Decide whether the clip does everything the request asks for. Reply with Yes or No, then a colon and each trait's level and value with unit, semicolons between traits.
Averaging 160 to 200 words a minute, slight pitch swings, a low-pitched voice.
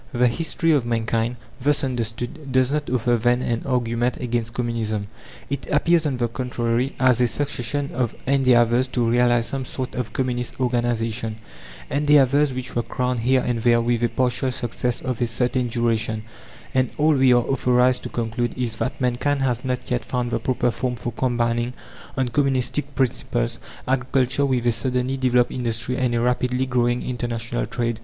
Yes: average, 170 wpm; narrow, 1.7 semitones; low, 125 Hz